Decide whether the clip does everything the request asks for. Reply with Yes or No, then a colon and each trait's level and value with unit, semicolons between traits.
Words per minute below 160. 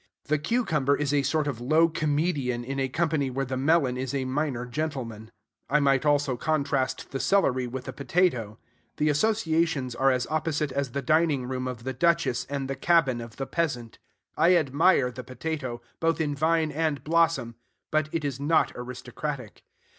No: average, 175 wpm